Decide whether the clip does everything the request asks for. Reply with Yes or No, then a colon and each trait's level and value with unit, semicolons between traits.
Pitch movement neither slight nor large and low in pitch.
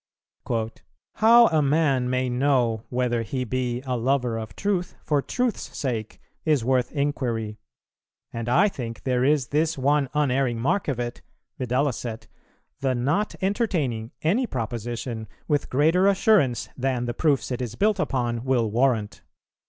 Yes: average, 3.8 semitones; low, 130 Hz